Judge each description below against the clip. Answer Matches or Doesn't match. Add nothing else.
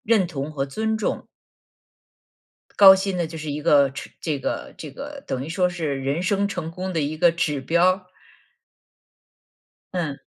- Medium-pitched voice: Matches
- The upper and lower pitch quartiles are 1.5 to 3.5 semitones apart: Doesn't match